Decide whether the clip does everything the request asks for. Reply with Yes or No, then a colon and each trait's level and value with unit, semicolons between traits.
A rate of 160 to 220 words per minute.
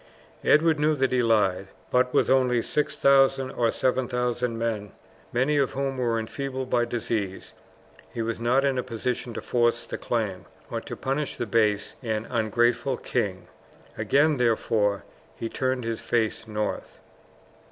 No: average, 150 wpm